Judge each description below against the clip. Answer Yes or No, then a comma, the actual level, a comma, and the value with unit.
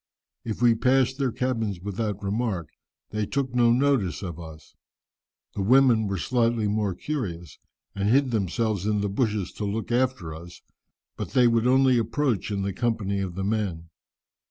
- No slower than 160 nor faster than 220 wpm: Yes, average, 165 wpm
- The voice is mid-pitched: No, low, 110 Hz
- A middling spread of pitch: Yes, average, 4.1 semitones